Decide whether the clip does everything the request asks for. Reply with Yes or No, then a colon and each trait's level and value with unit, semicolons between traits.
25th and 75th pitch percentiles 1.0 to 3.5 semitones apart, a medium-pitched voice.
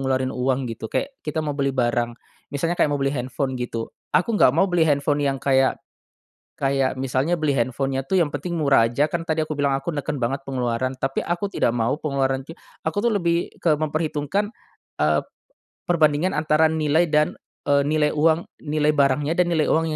Yes: average, 3.1 semitones; medium, 145 Hz